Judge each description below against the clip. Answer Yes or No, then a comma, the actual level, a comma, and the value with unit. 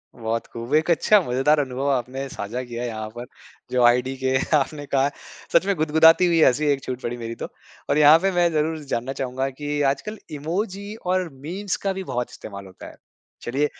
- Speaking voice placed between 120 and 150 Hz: Yes, medium, 140 Hz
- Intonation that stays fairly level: No, average, 4.6 semitones